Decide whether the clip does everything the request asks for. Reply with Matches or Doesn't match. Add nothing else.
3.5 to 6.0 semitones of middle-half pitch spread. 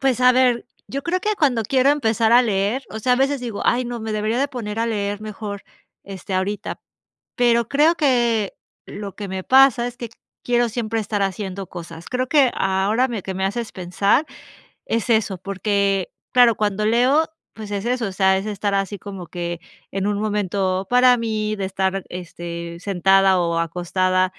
Matches